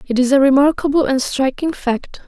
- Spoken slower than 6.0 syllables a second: Yes, 5.2 syllables/s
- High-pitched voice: Yes, very high, 275 Hz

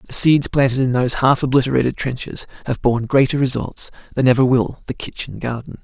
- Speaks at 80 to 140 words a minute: No, average, 185 wpm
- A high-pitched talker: No, low, 130 Hz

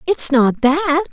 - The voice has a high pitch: Yes, very high, 305 Hz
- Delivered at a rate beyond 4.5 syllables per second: No, 4.4 syllables/s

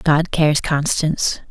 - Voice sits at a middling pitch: Yes, medium, 155 Hz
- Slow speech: Yes, slow, 120 wpm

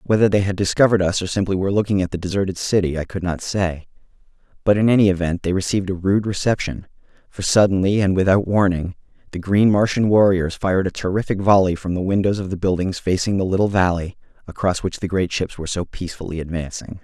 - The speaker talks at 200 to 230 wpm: Yes, fast, 205 wpm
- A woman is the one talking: No, male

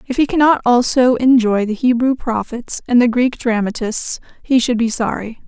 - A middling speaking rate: Yes, average, 175 wpm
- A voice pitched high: Yes, high, 240 Hz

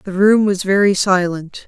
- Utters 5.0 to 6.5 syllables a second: No, 4.3 syllables/s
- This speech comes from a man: No, female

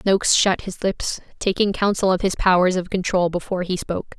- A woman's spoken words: Yes, female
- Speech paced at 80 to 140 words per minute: No, average, 200 wpm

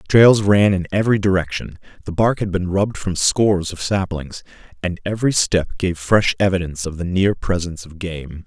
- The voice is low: Yes, very low, 95 Hz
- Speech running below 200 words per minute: Yes, average, 185 wpm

